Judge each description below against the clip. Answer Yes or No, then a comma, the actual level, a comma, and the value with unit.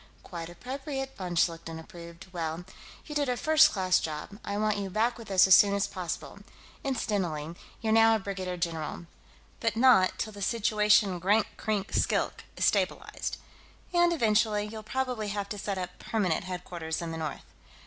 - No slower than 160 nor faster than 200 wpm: Yes, average, 175 wpm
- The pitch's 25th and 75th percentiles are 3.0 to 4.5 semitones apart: Yes, average, 4.0 semitones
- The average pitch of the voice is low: No, high, 200 Hz